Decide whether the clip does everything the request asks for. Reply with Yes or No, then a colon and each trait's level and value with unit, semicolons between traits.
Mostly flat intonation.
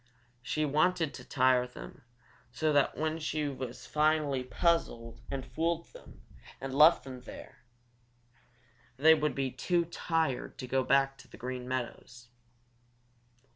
No: average, 3.6 semitones